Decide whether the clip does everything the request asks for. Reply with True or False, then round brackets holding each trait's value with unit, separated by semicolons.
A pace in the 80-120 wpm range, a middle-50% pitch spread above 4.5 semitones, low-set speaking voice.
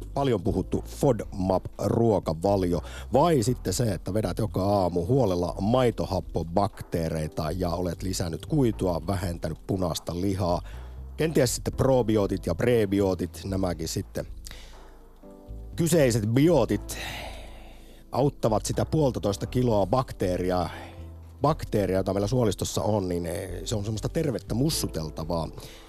True (100 wpm; 5.0 semitones; 100 Hz)